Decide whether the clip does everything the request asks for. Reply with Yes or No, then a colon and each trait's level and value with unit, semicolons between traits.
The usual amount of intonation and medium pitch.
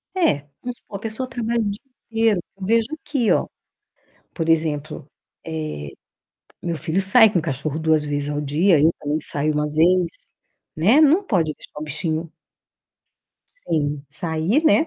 No: wide, 6.5 semitones; medium, 165 Hz